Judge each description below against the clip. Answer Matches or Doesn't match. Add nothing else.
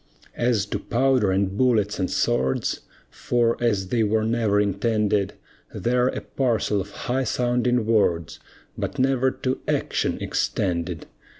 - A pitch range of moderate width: Matches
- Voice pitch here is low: Matches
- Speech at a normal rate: Doesn't match